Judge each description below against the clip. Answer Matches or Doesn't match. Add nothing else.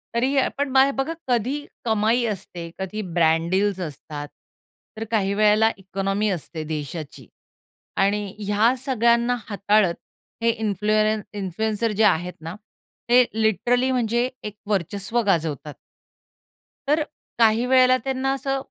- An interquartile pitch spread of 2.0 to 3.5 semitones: Doesn't match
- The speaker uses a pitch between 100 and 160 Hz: Doesn't match